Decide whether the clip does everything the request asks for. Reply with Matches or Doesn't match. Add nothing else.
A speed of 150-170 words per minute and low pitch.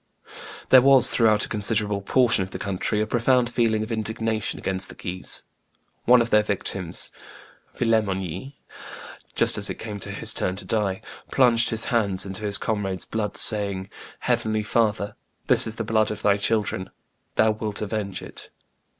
Matches